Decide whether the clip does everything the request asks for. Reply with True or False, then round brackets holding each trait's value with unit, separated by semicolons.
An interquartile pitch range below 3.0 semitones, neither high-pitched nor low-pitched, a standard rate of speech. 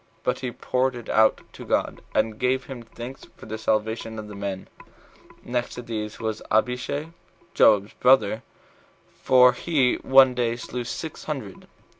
False (2.6 semitones; 120 Hz; 160 wpm)